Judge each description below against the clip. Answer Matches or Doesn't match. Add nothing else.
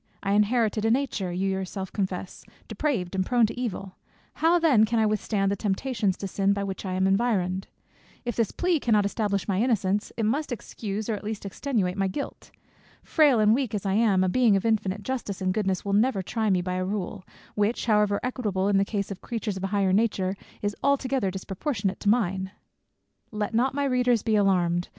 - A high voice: Matches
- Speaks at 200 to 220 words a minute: Matches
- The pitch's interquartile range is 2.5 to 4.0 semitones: Matches